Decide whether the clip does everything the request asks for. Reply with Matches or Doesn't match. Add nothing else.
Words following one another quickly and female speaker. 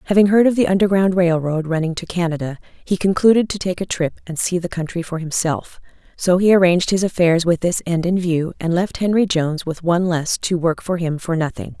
Matches